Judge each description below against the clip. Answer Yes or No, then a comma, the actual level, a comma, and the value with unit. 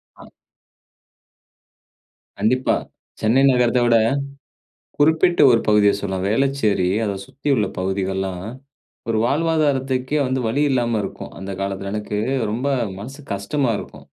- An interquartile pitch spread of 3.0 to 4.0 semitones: No, average, 5.2 semitones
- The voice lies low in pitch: Yes, low, 115 Hz